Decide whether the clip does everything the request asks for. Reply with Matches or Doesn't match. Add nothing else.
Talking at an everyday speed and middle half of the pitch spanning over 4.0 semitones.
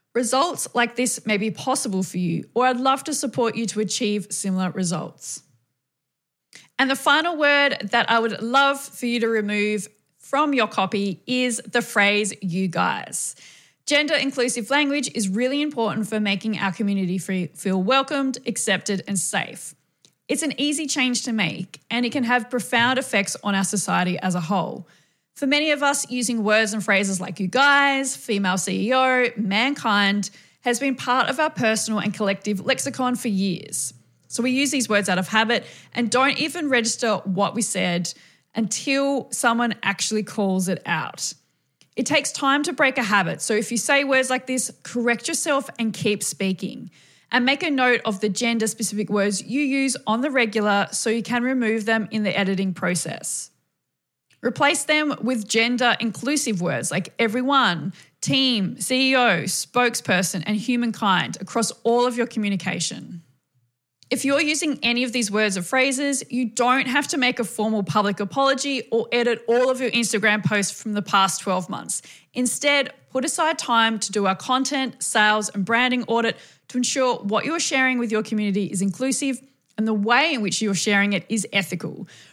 Matches